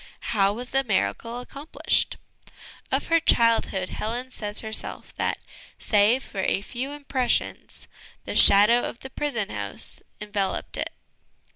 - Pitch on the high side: Yes, high, 230 Hz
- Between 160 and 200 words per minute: No, slow, 135 wpm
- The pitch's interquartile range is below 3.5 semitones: No, average, 3.9 semitones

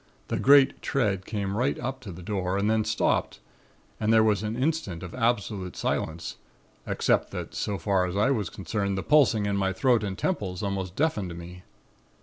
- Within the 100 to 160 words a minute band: No, average, 185 wpm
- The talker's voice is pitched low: Yes, low, 105 Hz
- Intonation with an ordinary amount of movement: Yes, average, 3.7 semitones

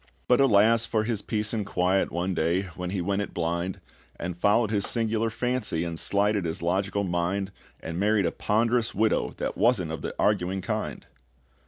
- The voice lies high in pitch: No, low, 100 Hz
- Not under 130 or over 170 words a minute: No, average, 180 wpm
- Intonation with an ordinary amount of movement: Yes, average, 3.7 semitones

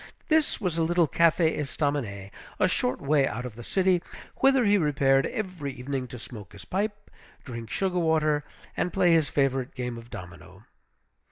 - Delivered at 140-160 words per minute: No, average, 170 wpm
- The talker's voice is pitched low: No, medium, 145 Hz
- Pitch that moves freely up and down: Yes, wide, 6.2 semitones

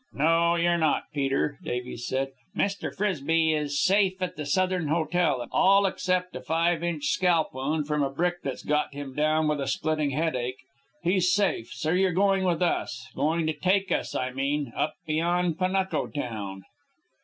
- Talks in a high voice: No, medium, 160 Hz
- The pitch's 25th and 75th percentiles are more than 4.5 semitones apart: No, average, 3.9 semitones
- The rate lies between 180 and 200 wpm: No, average, 170 wpm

